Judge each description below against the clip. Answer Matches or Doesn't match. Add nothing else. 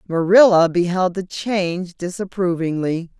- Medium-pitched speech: Matches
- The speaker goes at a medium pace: Doesn't match